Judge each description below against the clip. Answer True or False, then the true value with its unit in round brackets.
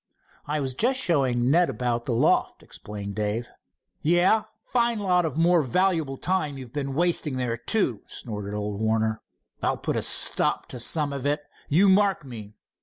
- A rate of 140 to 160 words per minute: False (170 wpm)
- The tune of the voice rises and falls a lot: True (7.1 semitones)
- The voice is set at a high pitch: False (140 Hz)